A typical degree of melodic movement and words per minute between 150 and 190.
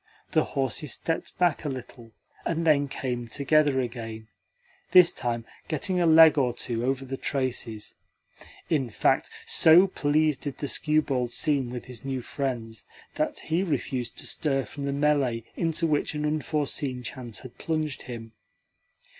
Yes: average, 3.9 semitones; average, 155 wpm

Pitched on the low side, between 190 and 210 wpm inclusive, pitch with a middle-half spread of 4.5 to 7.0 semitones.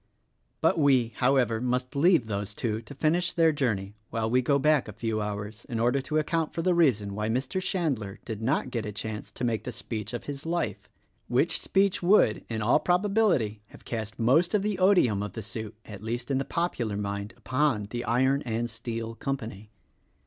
Yes: low, 120 Hz; average, 200 wpm; wide, 5.6 semitones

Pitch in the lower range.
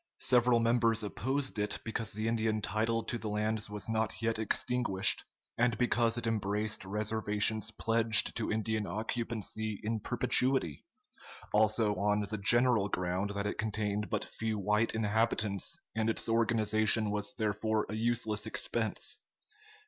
Yes: low, 110 Hz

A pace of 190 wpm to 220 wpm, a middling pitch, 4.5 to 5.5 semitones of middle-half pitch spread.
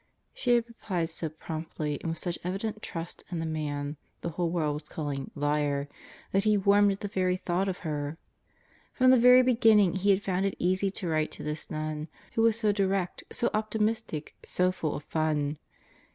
Yes: average, 195 wpm; medium, 180 Hz; average, 4.8 semitones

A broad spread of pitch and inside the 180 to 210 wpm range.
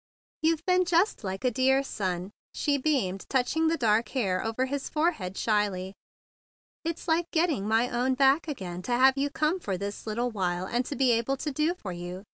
Yes: wide, 7.2 semitones; average, 200 wpm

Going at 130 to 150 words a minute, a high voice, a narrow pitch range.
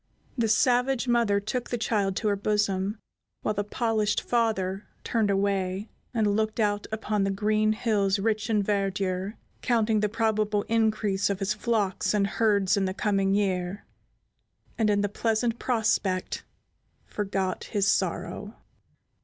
Yes: average, 145 wpm; high, 210 Hz; narrow, 2.0 semitones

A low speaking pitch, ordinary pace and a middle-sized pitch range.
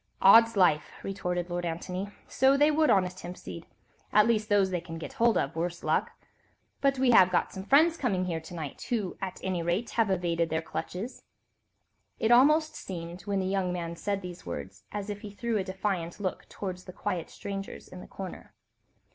No: high, 190 Hz; average, 190 wpm; average, 3.4 semitones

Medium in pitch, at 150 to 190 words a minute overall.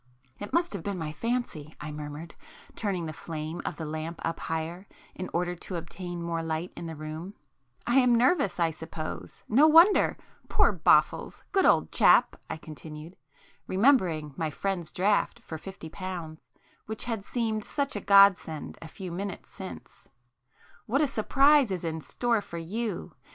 Yes: medium, 175 Hz; average, 160 wpm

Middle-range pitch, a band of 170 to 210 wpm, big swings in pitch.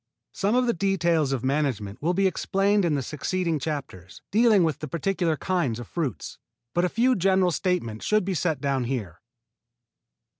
Yes: medium, 165 Hz; average, 175 wpm; wide, 6.0 semitones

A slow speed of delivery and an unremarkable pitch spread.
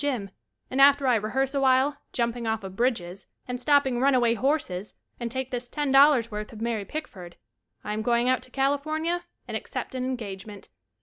No: average, 195 wpm; average, 3.7 semitones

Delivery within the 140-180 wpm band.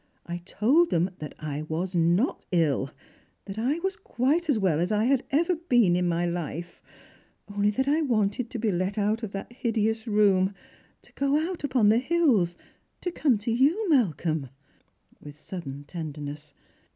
Yes: average, 175 wpm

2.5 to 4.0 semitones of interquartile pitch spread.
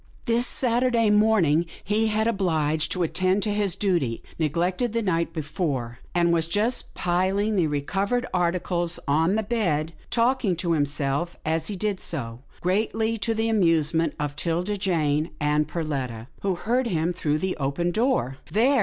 No: wide, 5.4 semitones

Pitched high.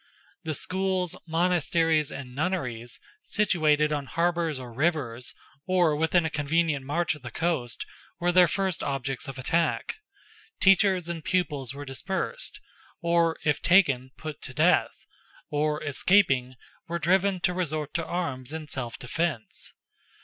No: medium, 160 Hz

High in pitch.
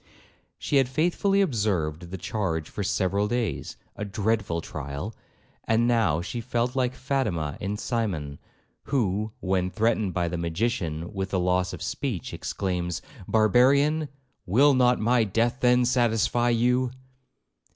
No: low, 110 Hz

